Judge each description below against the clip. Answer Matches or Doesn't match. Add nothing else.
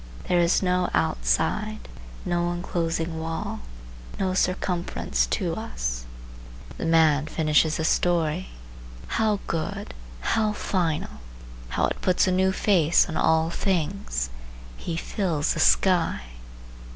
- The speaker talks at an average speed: Doesn't match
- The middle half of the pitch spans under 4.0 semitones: Matches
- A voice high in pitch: Doesn't match